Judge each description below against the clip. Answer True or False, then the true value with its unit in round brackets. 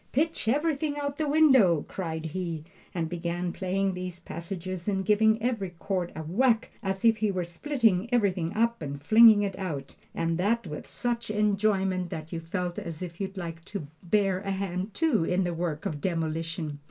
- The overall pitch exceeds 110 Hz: True (185 Hz)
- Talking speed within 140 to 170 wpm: False (185 wpm)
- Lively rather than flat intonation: False (4.4 semitones)